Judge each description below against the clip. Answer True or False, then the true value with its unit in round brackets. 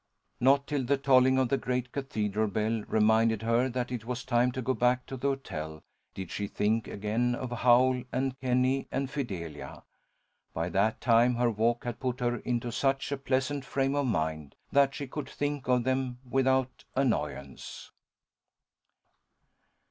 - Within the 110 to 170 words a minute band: True (165 wpm)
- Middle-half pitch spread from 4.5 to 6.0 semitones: False (2.9 semitones)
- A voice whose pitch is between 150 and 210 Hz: False (125 Hz)